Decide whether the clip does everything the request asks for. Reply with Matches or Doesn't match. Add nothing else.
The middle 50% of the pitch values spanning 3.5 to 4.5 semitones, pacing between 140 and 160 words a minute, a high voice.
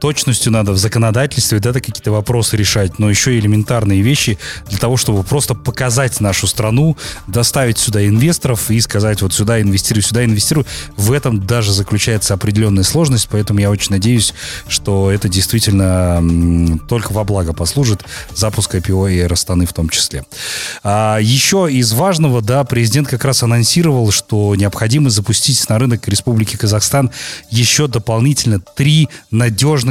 Doesn't match